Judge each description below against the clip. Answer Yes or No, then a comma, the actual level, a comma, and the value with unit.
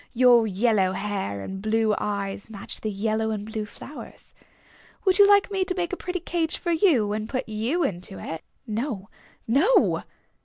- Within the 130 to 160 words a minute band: No, average, 170 wpm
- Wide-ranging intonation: Yes, wide, 7.8 semitones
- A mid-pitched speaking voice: No, high, 220 Hz